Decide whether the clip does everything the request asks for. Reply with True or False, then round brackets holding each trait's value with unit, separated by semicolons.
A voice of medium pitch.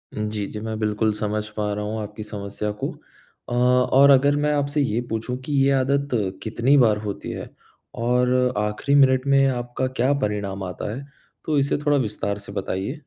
False (115 Hz)